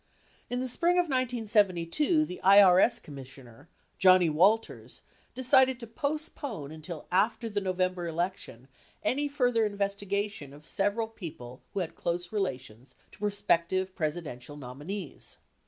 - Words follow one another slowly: Yes, slow, 120 wpm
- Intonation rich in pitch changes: Yes, wide, 6.2 semitones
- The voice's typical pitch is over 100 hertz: Yes, high, 190 Hz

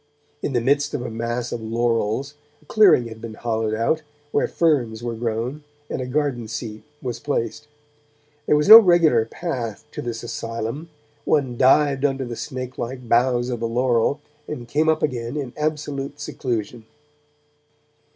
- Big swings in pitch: No, average, 3.9 semitones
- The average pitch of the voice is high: No, low, 125 Hz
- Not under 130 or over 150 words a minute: No, average, 160 wpm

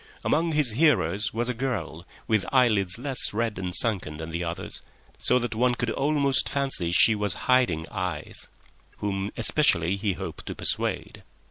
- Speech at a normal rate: Yes, average, 160 wpm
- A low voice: Yes, low, 110 Hz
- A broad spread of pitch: Yes, wide, 5.8 semitones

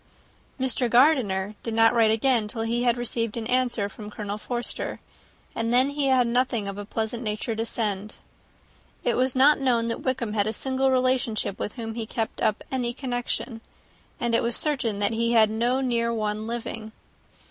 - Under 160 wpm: No, average, 185 wpm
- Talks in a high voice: Yes, high, 235 Hz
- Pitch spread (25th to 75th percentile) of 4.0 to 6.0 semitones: No, narrow, 2.4 semitones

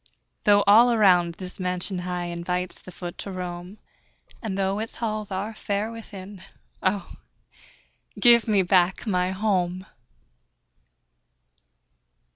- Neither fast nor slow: No, slow, 115 wpm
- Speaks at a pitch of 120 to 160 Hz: No, high, 190 Hz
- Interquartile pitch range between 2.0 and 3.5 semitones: Yes, narrow, 2.5 semitones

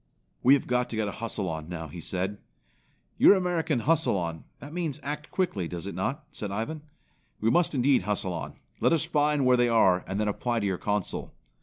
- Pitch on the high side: No, low, 115 Hz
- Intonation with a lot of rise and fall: Yes, wide, 7.6 semitones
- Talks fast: Yes, fast, 210 wpm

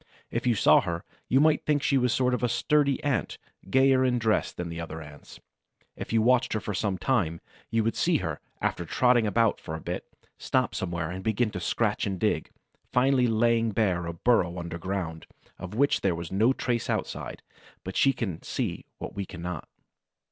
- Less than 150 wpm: No, average, 190 wpm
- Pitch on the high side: No, low, 110 Hz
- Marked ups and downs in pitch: Yes, wide, 6.0 semitones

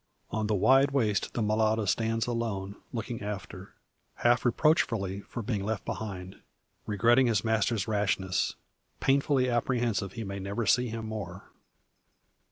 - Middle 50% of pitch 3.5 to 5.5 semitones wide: No, average, 3.1 semitones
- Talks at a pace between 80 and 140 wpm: Yes, slow, 135 wpm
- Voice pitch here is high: No, low, 110 Hz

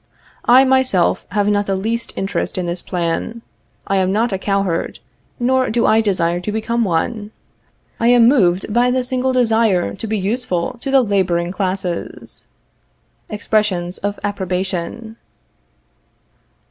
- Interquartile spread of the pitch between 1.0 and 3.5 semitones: No, average, 4.1 semitones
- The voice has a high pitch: Yes, high, 205 Hz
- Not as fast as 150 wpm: Yes, average, 140 wpm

